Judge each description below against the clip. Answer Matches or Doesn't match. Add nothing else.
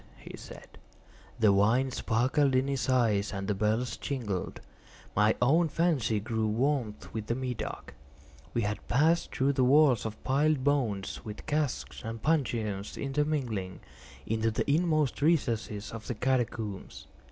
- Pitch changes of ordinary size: Matches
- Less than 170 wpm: Matches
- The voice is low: Matches